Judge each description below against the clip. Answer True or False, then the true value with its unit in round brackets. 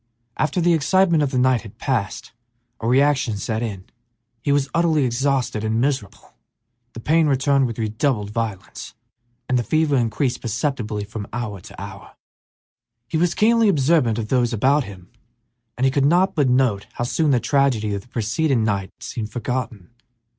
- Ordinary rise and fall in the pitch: True (4.7 semitones)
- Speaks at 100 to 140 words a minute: False (170 wpm)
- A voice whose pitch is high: False (125 Hz)